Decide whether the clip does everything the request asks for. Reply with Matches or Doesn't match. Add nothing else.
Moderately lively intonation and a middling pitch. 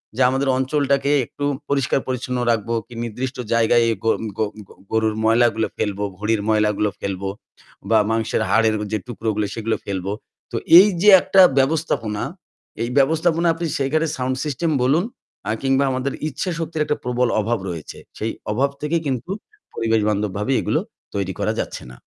Doesn't match